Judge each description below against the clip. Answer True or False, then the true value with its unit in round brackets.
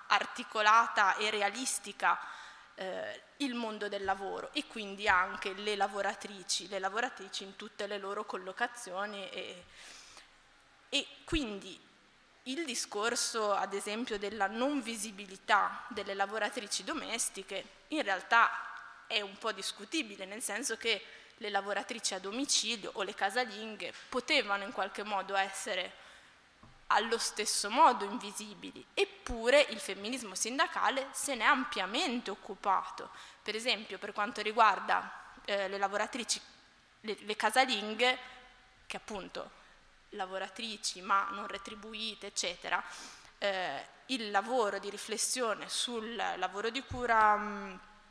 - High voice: True (210 Hz)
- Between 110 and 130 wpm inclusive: True (120 wpm)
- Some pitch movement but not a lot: True (3.2 semitones)